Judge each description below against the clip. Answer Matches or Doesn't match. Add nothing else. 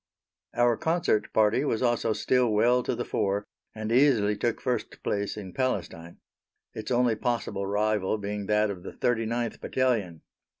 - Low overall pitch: Matches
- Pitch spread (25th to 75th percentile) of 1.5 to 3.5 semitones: Matches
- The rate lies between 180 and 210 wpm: Doesn't match